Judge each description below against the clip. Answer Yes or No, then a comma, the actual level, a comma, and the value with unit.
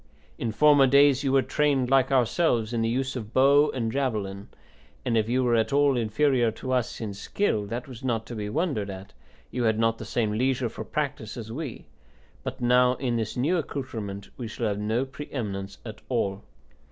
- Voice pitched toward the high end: No, low, 120 Hz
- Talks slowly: No, average, 200 wpm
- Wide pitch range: No, average, 3.5 semitones